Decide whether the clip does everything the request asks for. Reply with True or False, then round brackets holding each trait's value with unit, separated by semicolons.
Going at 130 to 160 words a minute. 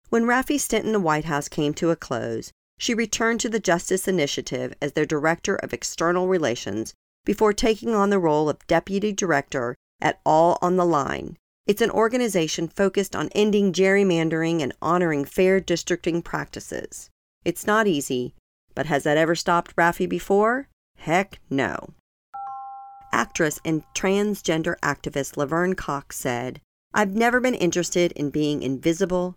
True (150 wpm)